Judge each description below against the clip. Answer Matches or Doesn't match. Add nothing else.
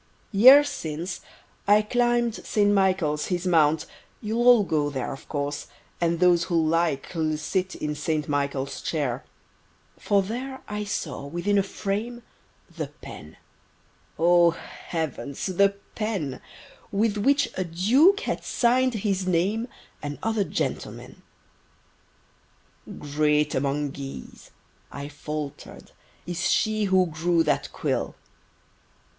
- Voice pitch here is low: Doesn't match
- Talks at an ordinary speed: Doesn't match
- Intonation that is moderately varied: Doesn't match